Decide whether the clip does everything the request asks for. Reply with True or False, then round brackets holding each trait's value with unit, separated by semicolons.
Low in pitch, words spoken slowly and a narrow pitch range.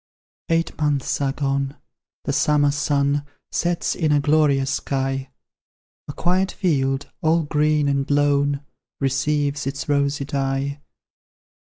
False (145 Hz; 120 wpm; 1.5 semitones)